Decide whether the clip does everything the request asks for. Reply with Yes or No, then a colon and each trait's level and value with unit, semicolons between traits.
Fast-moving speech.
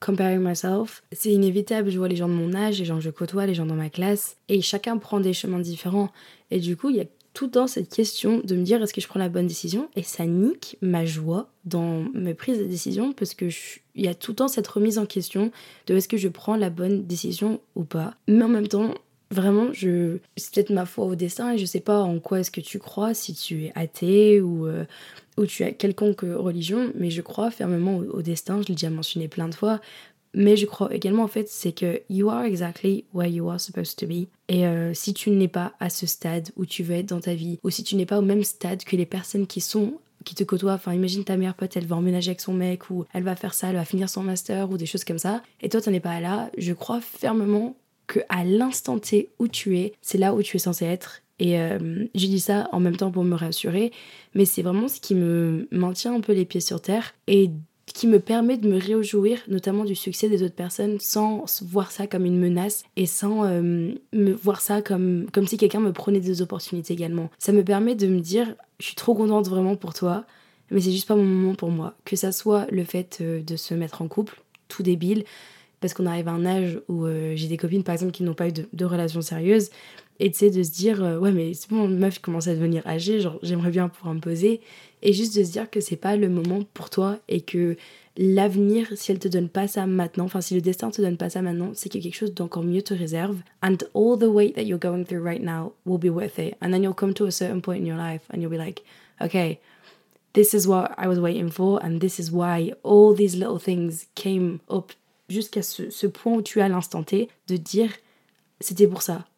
Yes: fast, 250 wpm